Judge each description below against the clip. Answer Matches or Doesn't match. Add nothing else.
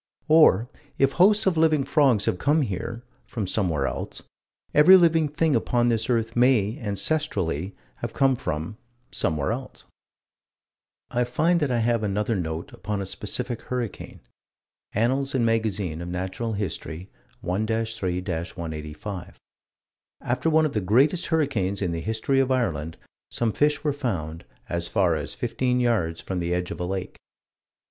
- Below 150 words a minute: Doesn't match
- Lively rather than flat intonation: Matches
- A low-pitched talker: Matches